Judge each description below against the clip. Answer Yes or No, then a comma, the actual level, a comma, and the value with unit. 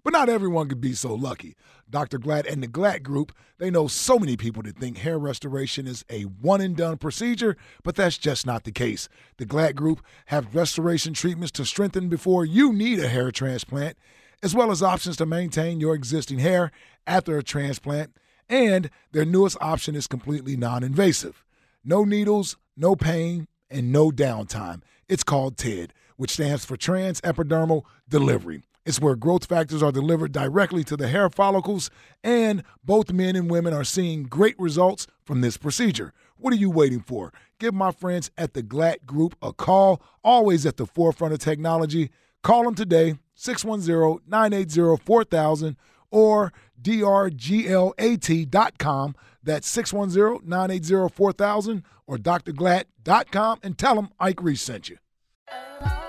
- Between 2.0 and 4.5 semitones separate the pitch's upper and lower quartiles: No, average, 5.2 semitones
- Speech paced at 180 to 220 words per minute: No, average, 155 wpm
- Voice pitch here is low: No, medium, 165 Hz